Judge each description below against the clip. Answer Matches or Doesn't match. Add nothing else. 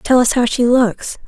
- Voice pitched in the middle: Doesn't match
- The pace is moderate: Doesn't match